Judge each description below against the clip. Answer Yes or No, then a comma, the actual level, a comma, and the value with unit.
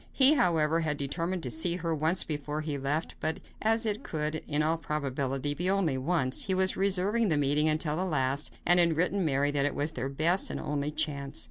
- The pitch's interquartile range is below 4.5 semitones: Yes, average, 3.6 semitones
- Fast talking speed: Yes, fast, 220 wpm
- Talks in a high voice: No, medium, 155 Hz